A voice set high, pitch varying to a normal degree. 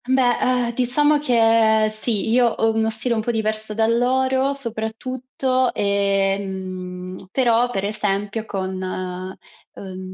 Yes: high, 225 Hz; average, 3.7 semitones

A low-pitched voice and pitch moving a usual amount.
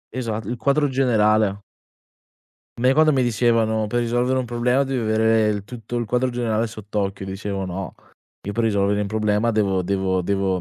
Yes: low, 110 Hz; average, 3.1 semitones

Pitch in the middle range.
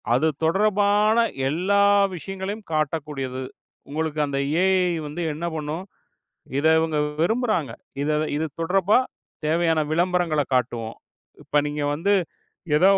Yes: medium, 160 Hz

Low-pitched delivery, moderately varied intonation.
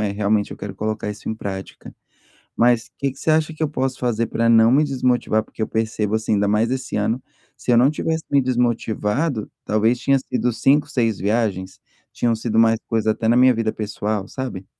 Yes: low, 115 Hz; average, 3.1 semitones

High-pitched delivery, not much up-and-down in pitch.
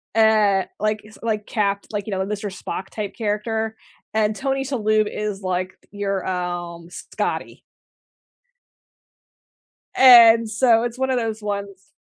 Yes: high, 210 Hz; narrow, 2.1 semitones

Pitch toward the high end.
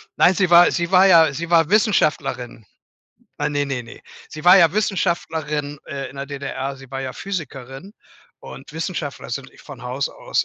No: medium, 155 Hz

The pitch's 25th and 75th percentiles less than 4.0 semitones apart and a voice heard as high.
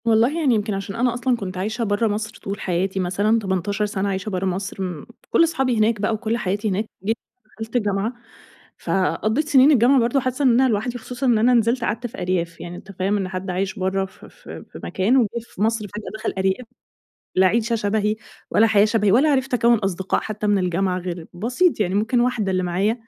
Yes: average, 3.6 semitones; high, 215 Hz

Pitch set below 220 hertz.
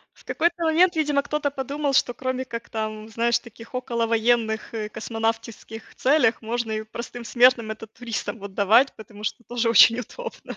No: high, 235 Hz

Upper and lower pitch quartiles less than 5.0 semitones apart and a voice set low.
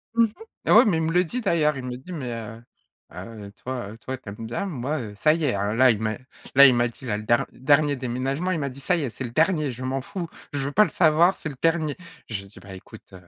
No: wide, 5.5 semitones; low, 130 Hz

